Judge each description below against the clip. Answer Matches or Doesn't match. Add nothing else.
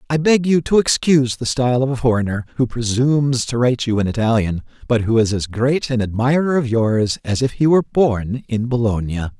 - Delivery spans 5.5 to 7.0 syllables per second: Matches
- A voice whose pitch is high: Doesn't match